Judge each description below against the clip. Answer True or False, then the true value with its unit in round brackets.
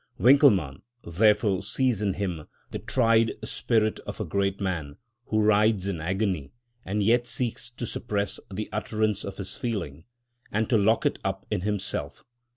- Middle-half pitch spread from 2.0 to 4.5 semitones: True (2.8 semitones)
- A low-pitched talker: True (105 Hz)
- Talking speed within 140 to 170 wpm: True (160 wpm)